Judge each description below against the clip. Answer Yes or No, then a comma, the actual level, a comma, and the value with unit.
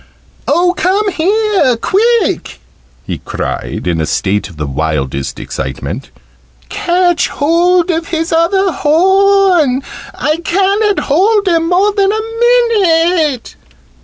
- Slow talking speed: Yes, slow, 115 wpm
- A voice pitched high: Yes, very high, 350 Hz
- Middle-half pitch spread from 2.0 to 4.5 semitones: No, average, 4.9 semitones